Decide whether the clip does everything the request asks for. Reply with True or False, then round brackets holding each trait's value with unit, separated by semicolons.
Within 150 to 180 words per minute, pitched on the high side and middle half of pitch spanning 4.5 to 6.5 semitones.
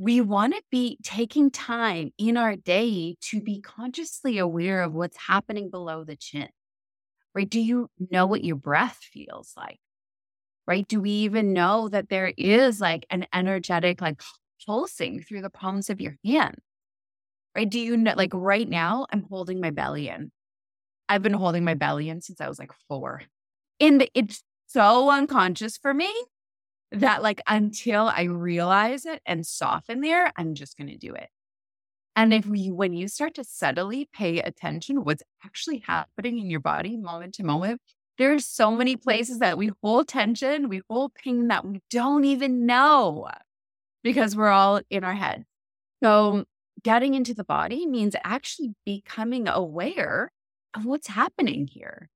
True (170 wpm; 210 Hz; 5.6 semitones)